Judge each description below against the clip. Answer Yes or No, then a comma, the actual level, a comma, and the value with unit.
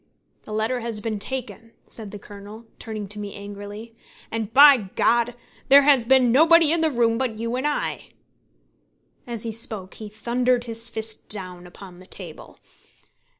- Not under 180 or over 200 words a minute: No, average, 165 wpm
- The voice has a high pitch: Yes, high, 225 Hz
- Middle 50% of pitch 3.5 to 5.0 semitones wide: No, average, 3.1 semitones